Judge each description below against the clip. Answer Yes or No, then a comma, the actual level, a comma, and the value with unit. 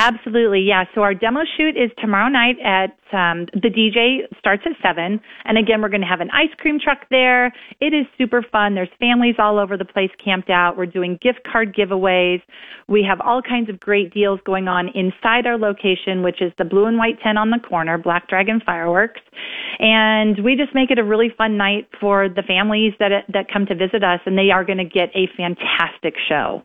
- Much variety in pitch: No, average, 3.8 semitones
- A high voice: Yes, high, 205 Hz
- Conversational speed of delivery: No, fast, 215 wpm